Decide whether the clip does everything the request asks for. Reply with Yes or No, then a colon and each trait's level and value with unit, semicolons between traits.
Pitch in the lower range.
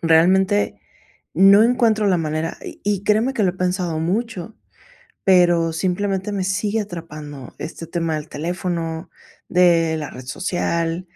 No: medium, 180 Hz